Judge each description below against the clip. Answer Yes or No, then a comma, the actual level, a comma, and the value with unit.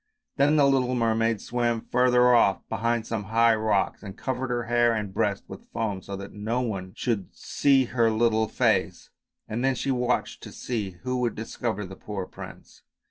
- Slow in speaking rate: No, average, 185 wpm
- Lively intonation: No, average, 2.8 semitones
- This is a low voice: Yes, low, 115 Hz